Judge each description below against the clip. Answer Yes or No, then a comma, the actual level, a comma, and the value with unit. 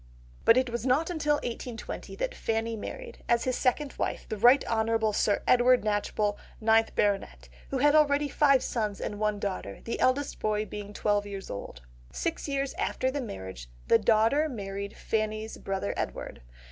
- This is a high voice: Yes, high, 225 Hz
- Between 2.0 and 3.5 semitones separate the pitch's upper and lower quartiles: No, average, 4.3 semitones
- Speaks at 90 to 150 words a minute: No, average, 170 wpm